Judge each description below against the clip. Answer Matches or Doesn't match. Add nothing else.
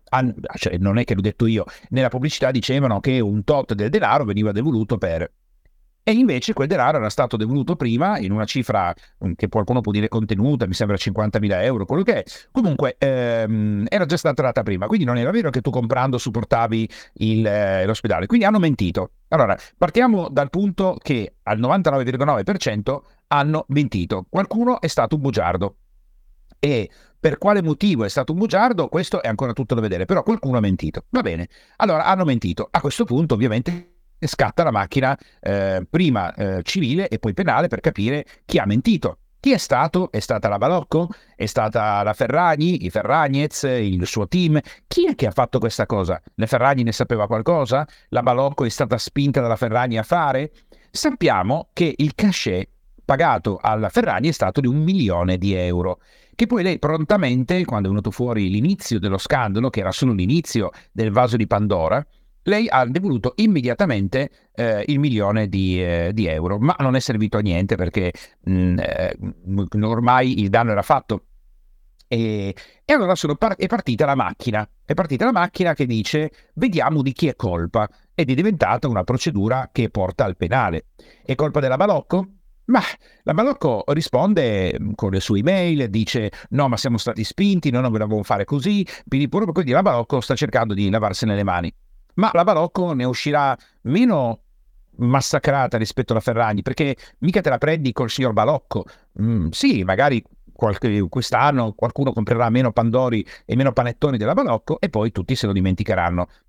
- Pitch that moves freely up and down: Matches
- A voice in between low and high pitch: Doesn't match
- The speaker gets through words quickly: Matches